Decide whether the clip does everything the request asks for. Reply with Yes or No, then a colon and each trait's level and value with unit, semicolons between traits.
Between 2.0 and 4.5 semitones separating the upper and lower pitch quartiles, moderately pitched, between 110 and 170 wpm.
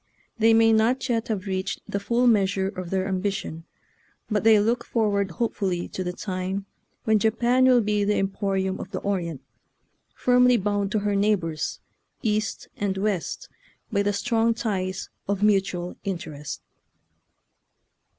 No: average, 2.7 semitones; high, 200 Hz; average, 150 wpm